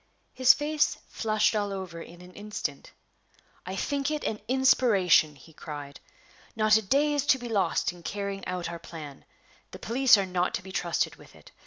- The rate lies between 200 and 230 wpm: No, average, 185 wpm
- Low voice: No, high, 200 Hz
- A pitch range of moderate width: No, wide, 6.0 semitones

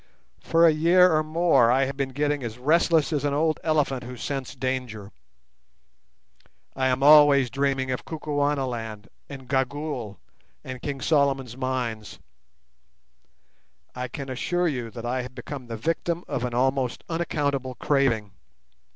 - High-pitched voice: No, low, 135 Hz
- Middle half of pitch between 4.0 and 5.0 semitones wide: No, average, 2.9 semitones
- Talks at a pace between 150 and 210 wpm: No, average, 140 wpm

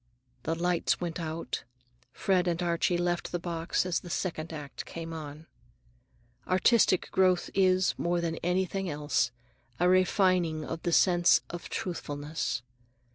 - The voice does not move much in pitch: Yes, narrow, 2.0 semitones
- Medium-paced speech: Yes, average, 145 wpm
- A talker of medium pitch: Yes, medium, 175 Hz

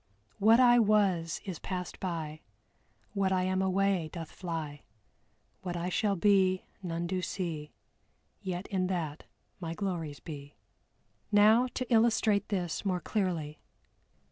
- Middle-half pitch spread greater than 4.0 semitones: No, average, 3.2 semitones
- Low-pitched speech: No, medium, 185 Hz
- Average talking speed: No, slow, 130 wpm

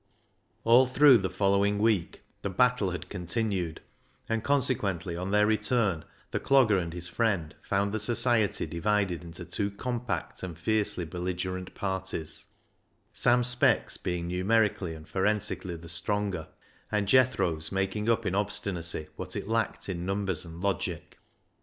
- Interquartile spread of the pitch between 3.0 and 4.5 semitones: Yes, average, 3.8 semitones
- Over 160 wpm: No, average, 140 wpm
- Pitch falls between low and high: No, low, 100 Hz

